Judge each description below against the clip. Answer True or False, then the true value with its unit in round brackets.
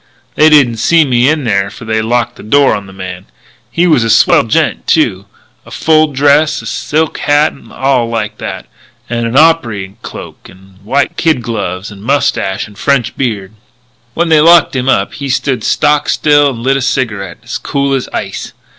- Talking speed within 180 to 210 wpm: True (190 wpm)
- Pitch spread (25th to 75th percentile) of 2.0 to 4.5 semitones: False (5.4 semitones)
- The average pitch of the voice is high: False (130 Hz)